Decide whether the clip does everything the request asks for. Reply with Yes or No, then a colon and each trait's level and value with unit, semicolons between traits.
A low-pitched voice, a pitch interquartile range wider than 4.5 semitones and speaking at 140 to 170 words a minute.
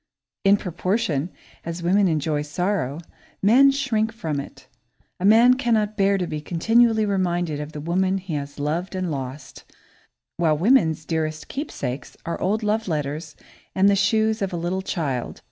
No: medium, 180 Hz; wide, 5.4 semitones; average, 160 wpm